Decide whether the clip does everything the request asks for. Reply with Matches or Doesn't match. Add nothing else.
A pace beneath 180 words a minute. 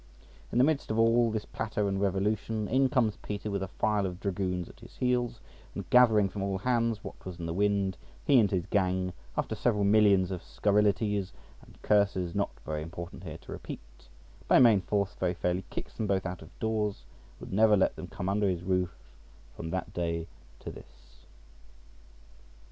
Doesn't match